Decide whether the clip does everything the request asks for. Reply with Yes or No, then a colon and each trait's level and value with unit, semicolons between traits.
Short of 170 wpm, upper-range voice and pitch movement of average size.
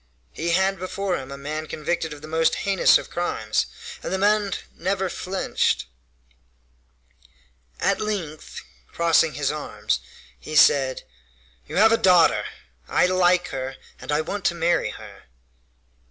No: average, 140 wpm; medium, 170 Hz; average, 4.2 semitones